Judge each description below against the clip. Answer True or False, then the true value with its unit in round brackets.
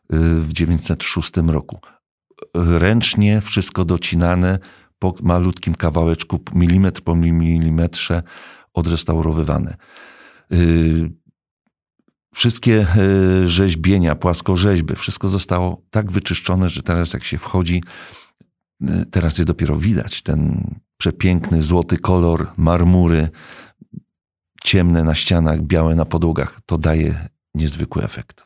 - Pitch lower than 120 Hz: True (85 Hz)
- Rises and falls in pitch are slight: True (2.0 semitones)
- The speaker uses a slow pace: True (95 wpm)